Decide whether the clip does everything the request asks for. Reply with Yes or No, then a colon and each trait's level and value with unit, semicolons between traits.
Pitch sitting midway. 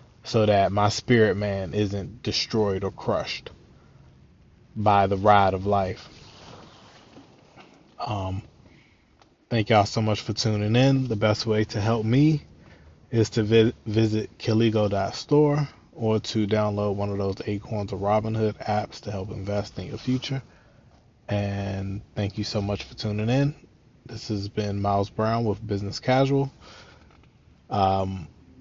No: low, 105 Hz